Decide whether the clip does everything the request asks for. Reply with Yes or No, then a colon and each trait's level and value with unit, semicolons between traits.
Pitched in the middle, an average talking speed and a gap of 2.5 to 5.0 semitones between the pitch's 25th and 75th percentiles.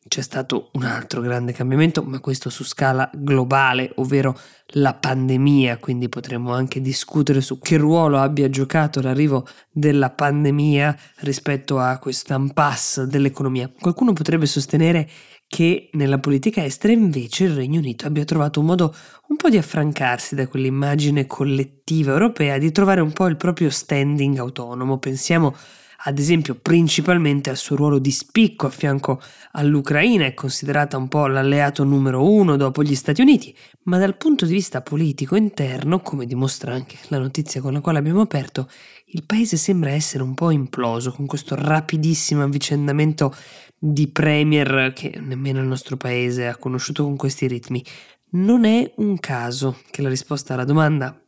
Yes: medium, 145 Hz; average, 155 wpm; average, 2.9 semitones